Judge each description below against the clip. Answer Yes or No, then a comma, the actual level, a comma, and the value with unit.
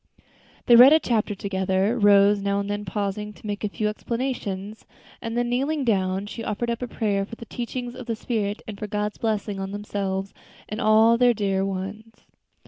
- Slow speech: No, average, 195 wpm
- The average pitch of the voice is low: No, high, 210 Hz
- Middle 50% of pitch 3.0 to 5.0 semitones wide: No, narrow, 2.6 semitones